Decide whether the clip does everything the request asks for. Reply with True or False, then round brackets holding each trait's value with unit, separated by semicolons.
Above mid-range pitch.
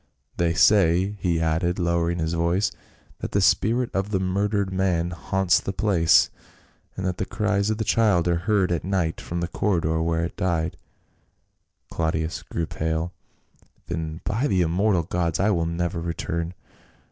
False (85 Hz)